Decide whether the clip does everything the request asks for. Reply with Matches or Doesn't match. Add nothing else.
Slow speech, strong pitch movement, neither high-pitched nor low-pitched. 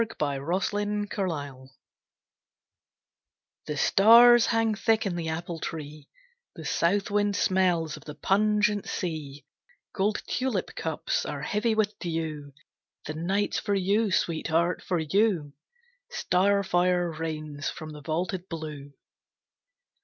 Doesn't match